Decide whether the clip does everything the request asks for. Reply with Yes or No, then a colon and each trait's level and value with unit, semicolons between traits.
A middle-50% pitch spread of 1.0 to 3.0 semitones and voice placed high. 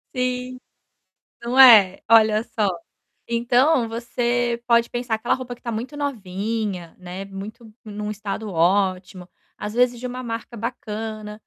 Yes: average, 2.7 semitones; high, 225 Hz